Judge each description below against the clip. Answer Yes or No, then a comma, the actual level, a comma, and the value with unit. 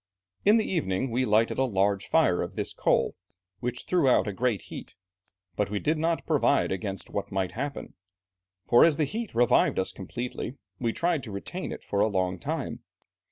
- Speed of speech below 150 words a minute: No, average, 190 wpm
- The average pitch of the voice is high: No, low, 120 Hz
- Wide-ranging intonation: Yes, wide, 6.7 semitones